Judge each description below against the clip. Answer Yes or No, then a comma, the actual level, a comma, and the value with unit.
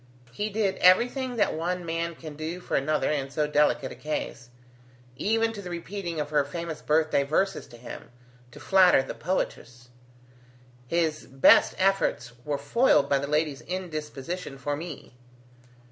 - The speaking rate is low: No, average, 155 wpm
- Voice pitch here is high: No, medium, 160 Hz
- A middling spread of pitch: Yes, average, 4.3 semitones